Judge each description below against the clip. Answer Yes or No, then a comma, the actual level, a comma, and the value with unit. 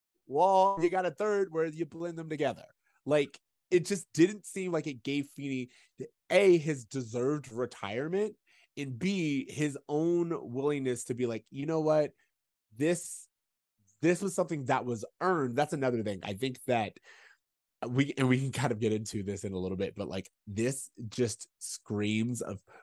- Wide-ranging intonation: Yes, wide, 5.8 semitones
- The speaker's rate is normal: Yes, average, 175 wpm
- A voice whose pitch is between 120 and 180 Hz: Yes, medium, 140 Hz